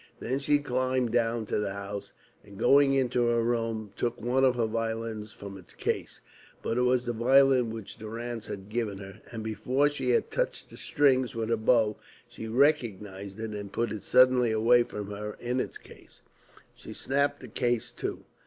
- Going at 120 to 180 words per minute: No, average, 190 wpm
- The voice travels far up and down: No, average, 2.9 semitones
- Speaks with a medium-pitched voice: No, low, 115 Hz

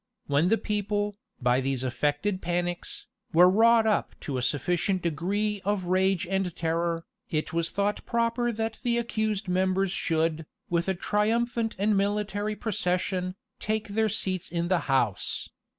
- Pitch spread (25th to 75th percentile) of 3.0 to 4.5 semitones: Yes, average, 3.7 semitones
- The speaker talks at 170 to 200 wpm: No, average, 150 wpm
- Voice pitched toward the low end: No, high, 190 Hz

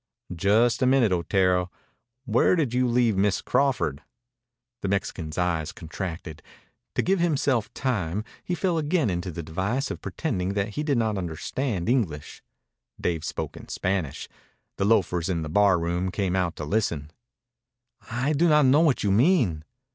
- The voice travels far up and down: Yes, wide, 6.7 semitones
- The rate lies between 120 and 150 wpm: No, average, 160 wpm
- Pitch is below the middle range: Yes, low, 100 Hz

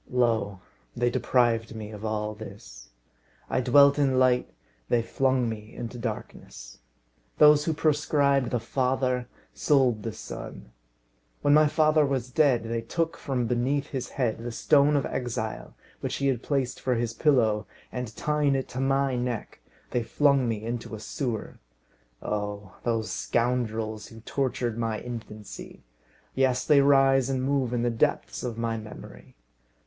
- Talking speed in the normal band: Yes, average, 155 wpm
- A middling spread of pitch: Yes, average, 3.3 semitones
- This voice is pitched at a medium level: No, low, 125 Hz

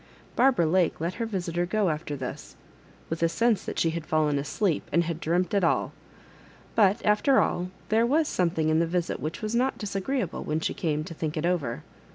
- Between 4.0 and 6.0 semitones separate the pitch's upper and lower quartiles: Yes, average, 4.7 semitones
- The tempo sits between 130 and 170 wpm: No, average, 200 wpm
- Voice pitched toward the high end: No, medium, 175 Hz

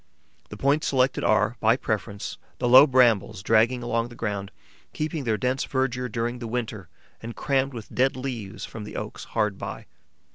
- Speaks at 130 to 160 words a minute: No, average, 175 wpm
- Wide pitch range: No, average, 3.1 semitones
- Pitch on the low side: Yes, low, 120 Hz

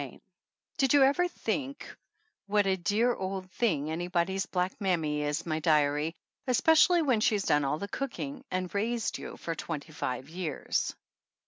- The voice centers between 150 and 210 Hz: Yes, medium, 185 Hz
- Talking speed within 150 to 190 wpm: Yes, average, 165 wpm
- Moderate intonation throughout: No, wide, 7.0 semitones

